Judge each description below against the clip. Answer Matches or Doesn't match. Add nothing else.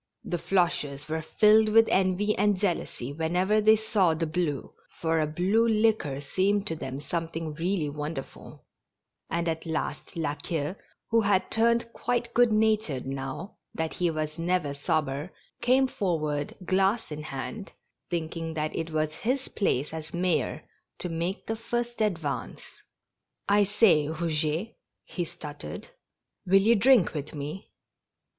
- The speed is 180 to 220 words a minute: Doesn't match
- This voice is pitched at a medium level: Matches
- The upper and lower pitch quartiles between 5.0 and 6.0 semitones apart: Matches